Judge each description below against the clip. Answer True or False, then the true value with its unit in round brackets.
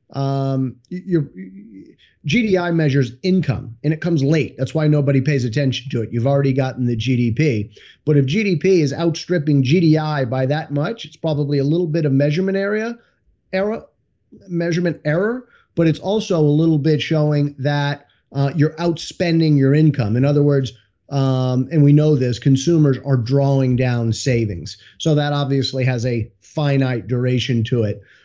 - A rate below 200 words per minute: True (160 wpm)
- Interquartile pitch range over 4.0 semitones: False (3.7 semitones)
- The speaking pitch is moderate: True (145 Hz)